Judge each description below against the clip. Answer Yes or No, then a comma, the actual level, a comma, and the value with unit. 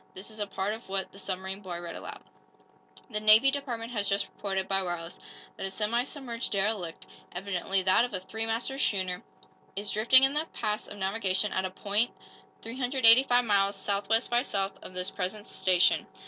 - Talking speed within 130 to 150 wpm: No, average, 185 wpm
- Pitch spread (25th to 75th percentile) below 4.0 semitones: Yes, average, 3.2 semitones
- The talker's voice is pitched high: Yes, high, 205 Hz